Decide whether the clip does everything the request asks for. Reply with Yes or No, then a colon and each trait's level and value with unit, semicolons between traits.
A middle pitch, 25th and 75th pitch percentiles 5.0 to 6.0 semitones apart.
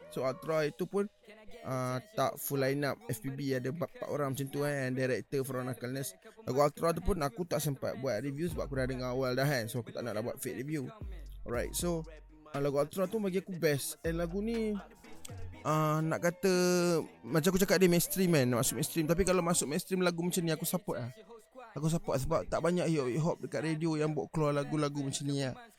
No: medium, 155 Hz; average, 4.6 semitones